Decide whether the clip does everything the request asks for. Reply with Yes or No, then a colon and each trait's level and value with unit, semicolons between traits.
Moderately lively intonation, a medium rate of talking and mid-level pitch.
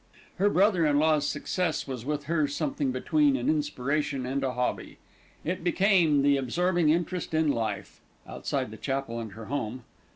Yes: average, 4.9 semitones; average, 165 wpm; medium, 150 Hz